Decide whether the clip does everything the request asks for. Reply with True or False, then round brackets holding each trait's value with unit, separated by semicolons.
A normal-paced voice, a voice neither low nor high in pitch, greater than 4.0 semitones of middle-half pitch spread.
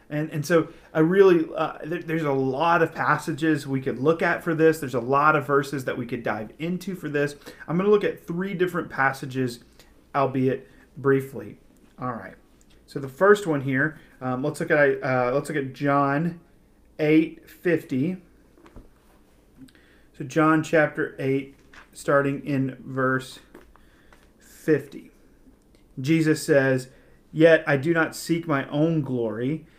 False (150 wpm; 150 Hz; 3.2 semitones)